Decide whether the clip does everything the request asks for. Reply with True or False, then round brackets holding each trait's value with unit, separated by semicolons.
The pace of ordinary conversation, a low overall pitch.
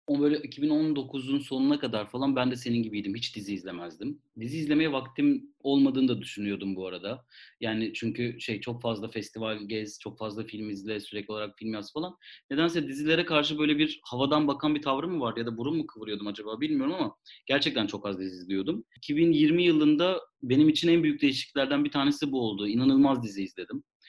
False (185 wpm; 130 Hz)